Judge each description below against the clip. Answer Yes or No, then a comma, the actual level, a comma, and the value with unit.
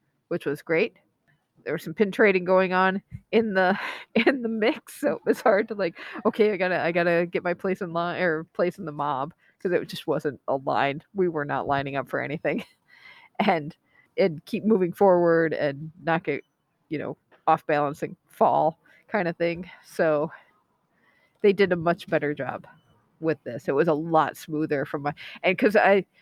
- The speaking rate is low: No, average, 190 wpm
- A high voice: No, medium, 170 Hz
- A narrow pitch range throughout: No, average, 3.8 semitones